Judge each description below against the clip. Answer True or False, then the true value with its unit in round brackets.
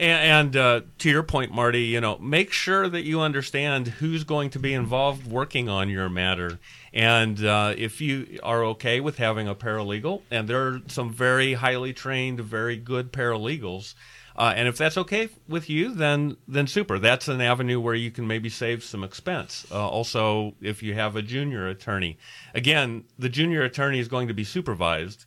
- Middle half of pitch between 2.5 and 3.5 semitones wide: False (4.1 semitones)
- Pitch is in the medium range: False (120 Hz)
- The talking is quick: False (190 wpm)